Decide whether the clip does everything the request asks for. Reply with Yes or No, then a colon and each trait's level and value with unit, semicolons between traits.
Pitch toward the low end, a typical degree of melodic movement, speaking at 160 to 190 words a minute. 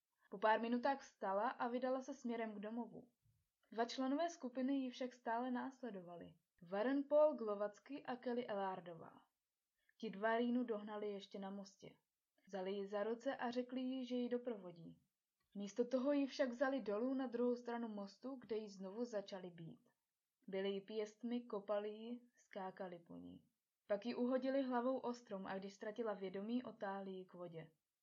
No: high, 225 Hz; average, 4.1 semitones; average, 165 wpm